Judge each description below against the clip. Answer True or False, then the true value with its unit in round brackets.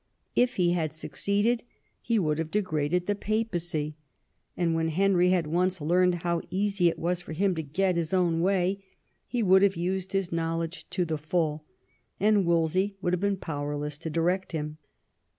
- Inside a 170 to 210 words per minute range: True (175 wpm)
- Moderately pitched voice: True (175 Hz)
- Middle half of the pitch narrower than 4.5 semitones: True (2.9 semitones)